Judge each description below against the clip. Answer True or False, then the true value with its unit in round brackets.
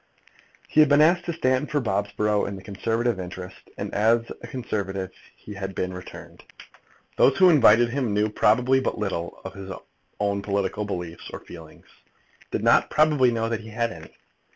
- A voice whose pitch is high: False (105 Hz)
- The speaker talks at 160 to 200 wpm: True (175 wpm)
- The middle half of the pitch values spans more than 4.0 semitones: True (4.6 semitones)